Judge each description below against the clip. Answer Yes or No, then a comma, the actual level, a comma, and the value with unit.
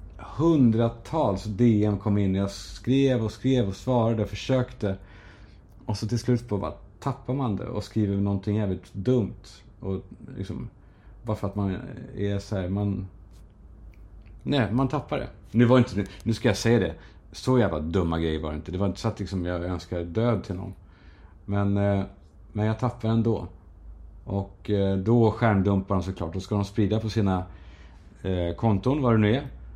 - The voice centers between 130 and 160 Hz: No, low, 100 Hz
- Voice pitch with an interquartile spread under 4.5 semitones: Yes, average, 3.3 semitones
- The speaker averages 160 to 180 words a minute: Yes, average, 175 wpm